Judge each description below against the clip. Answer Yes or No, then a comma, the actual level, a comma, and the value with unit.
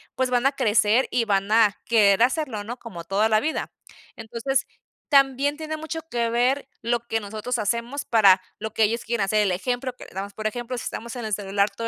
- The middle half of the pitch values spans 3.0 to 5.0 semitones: Yes, average, 3.3 semitones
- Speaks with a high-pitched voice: Yes, high, 230 Hz